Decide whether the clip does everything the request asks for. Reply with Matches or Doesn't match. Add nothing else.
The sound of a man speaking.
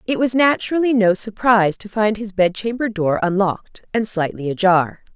Doesn't match